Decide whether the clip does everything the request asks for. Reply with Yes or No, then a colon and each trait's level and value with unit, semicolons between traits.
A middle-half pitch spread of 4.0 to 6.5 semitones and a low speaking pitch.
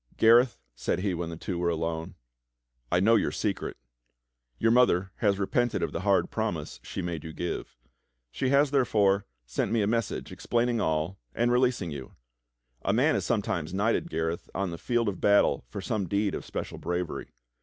Yes: average, 5.2 semitones; low, 100 Hz